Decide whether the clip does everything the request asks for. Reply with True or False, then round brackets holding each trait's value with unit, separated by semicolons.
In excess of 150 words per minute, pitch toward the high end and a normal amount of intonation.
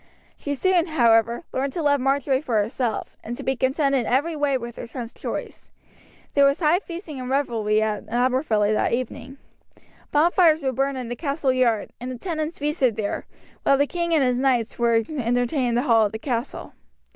True (190 wpm; 260 Hz; 3.6 semitones)